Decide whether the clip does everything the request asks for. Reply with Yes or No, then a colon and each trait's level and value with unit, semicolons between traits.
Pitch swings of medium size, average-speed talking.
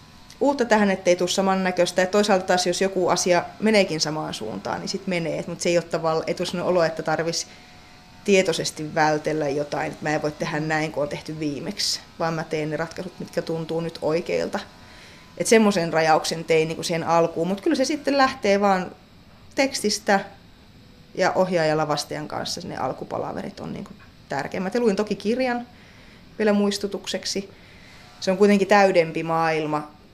No: average, 3.8 semitones; fast, 160 wpm